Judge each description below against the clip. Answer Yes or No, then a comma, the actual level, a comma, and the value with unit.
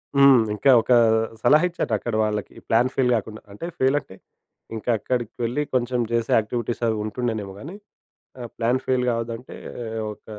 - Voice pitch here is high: No, low, 120 Hz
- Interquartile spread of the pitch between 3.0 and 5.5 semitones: No, narrow, 2.5 semitones